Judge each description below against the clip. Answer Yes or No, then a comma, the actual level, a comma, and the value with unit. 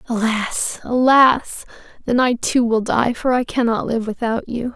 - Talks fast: No, average, 165 wpm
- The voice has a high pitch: Yes, high, 240 Hz